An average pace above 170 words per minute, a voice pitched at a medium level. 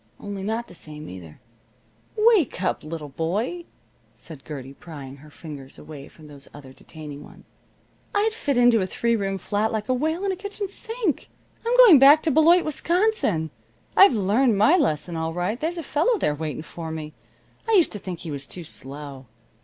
No: average, 185 wpm; high, 195 Hz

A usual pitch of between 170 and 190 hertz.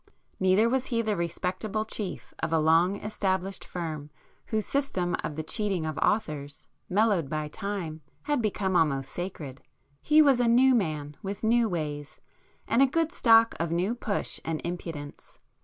Yes: medium, 185 Hz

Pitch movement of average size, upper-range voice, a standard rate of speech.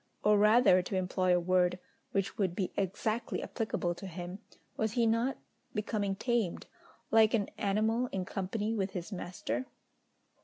Yes: average, 3.2 semitones; high, 200 Hz; average, 150 wpm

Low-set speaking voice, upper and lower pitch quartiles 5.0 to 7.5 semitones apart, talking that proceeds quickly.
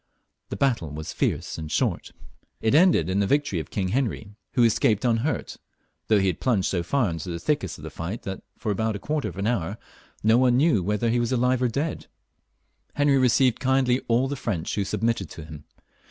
Yes: low, 115 Hz; wide, 5.4 semitones; fast, 210 wpm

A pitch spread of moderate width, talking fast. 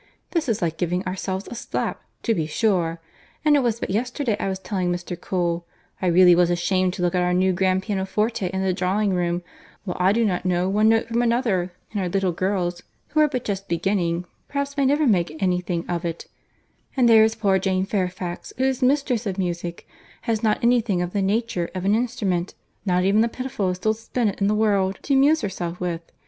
Yes: average, 4.0 semitones; fast, 215 wpm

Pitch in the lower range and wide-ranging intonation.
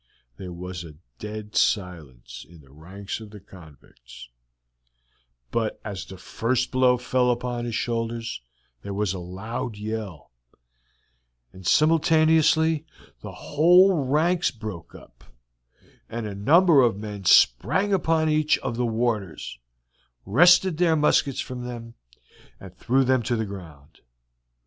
Yes: low, 115 Hz; wide, 6.4 semitones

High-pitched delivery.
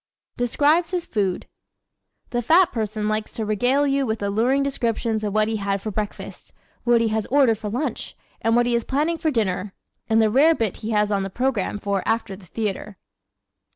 Yes: high, 225 Hz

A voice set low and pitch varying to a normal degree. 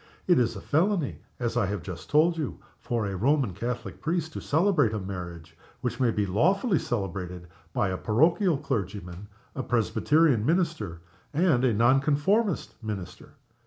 No: low, 120 Hz; wide, 8.0 semitones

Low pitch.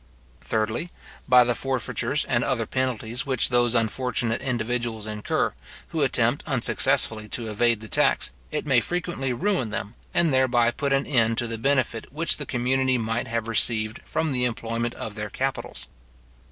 Yes: low, 120 Hz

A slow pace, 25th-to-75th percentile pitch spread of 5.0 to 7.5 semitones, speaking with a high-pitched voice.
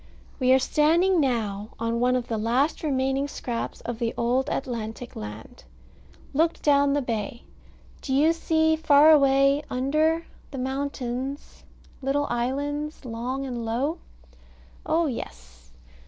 No: slow, 130 wpm; average, 3.6 semitones; very high, 265 Hz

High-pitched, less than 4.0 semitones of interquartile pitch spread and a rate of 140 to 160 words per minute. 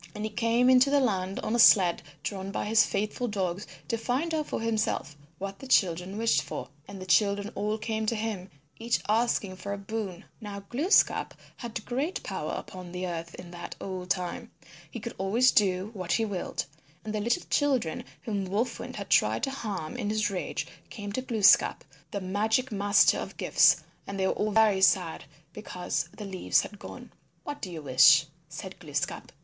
No: high, 205 Hz; average, 3.5 semitones; average, 190 wpm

